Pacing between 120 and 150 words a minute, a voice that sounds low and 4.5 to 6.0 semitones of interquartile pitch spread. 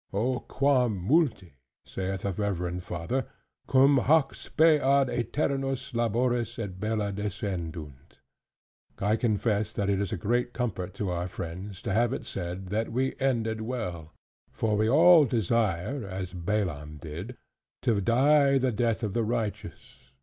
Yes: average, 145 wpm; low, 110 Hz; average, 5.2 semitones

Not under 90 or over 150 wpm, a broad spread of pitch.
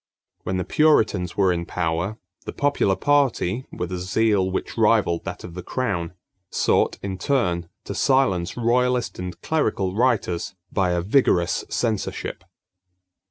Yes: average, 140 wpm; wide, 5.8 semitones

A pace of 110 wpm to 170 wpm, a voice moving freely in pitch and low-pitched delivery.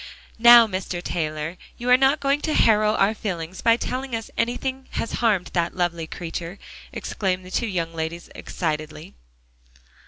No: average, 155 wpm; wide, 5.8 semitones; high, 190 Hz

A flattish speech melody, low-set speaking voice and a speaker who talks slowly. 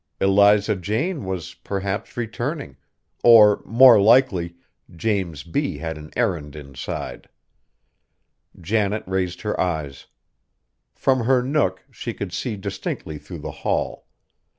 No: average, 4.9 semitones; low, 100 Hz; slow, 115 wpm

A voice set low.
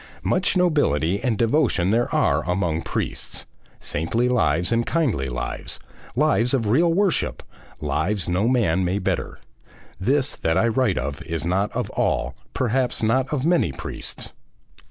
Yes: low, 110 Hz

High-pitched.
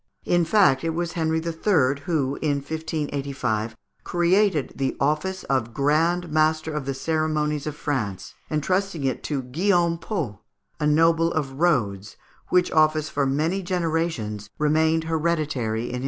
No: medium, 155 Hz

